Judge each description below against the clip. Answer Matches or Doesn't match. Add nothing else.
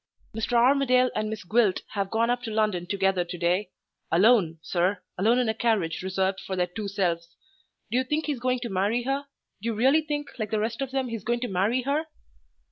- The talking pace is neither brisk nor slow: Doesn't match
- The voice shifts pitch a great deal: Doesn't match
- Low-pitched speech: Doesn't match